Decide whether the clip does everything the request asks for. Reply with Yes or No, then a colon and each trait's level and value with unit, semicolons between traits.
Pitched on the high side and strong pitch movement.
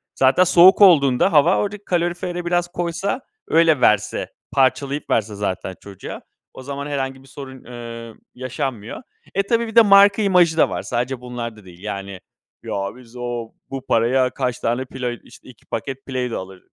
No: low, 130 Hz; wide, 6.6 semitones